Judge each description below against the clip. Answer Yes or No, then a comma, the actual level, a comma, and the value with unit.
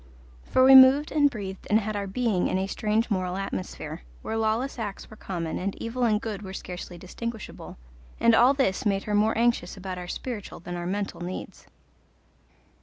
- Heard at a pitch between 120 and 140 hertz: No, high, 210 Hz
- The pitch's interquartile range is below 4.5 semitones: Yes, average, 3.7 semitones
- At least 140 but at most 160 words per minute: No, average, 185 wpm